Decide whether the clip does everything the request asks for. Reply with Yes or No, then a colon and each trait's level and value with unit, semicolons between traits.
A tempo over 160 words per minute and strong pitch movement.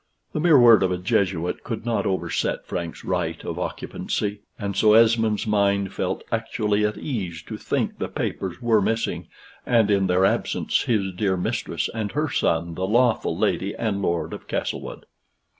No: average, 170 wpm; average, 3.2 semitones